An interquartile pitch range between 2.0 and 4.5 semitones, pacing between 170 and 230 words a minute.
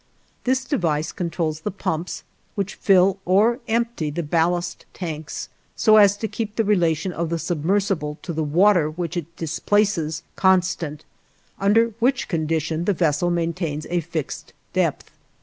No: average, 4.0 semitones; average, 145 wpm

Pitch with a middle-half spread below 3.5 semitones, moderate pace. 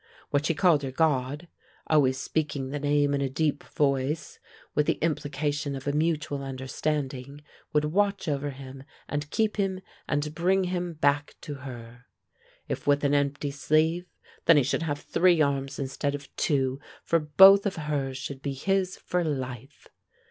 Yes: narrow, 2.6 semitones; average, 170 wpm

